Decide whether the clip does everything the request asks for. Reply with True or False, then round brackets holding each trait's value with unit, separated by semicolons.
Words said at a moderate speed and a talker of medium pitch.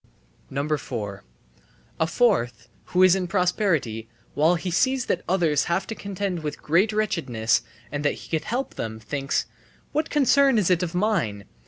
True (160 wpm; 175 Hz)